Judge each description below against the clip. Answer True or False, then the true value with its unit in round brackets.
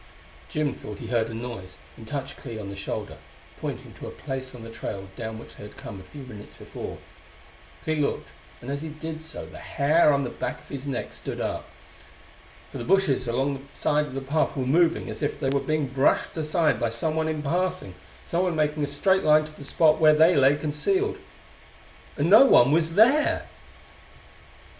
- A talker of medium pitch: True (145 Hz)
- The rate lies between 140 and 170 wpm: False (205 wpm)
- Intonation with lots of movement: False (4.2 semitones)